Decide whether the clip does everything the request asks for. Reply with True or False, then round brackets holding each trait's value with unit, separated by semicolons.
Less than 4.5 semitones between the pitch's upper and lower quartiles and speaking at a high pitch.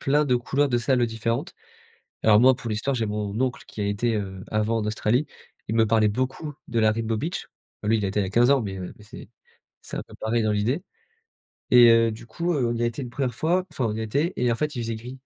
False (3.2 semitones; 115 Hz)